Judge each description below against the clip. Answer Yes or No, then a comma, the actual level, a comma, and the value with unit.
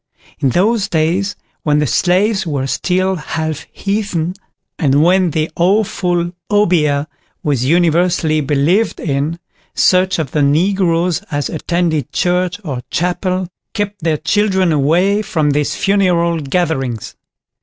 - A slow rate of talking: Yes, slow, 125 wpm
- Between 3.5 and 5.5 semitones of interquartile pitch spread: Yes, average, 3.8 semitones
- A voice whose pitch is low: No, medium, 170 Hz